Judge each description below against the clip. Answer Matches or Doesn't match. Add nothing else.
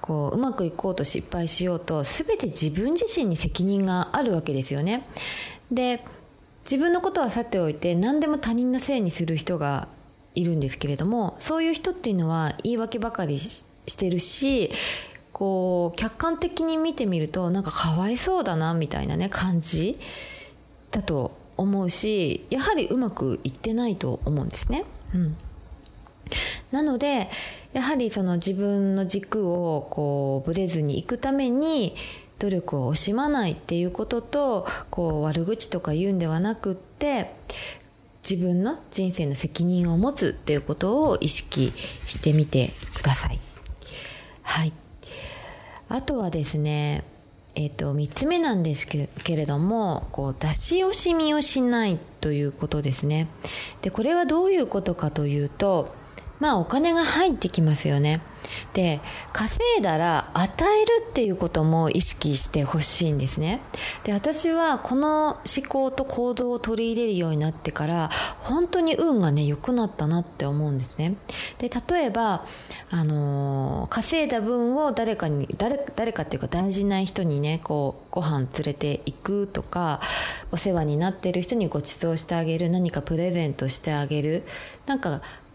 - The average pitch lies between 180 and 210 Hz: Matches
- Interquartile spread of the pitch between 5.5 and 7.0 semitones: Doesn't match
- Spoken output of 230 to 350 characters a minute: Matches